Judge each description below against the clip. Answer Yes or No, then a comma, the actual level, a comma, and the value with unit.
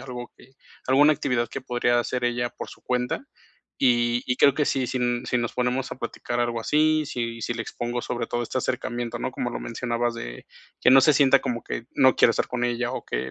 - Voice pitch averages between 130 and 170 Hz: No, low, 120 Hz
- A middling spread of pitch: No, narrow, 1.4 semitones